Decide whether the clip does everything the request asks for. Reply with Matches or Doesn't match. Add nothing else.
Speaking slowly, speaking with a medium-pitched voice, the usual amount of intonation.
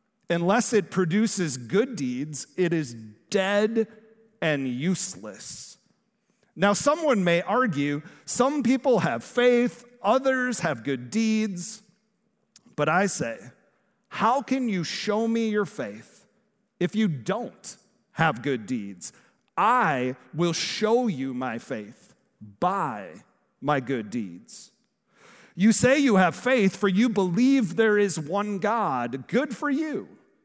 Doesn't match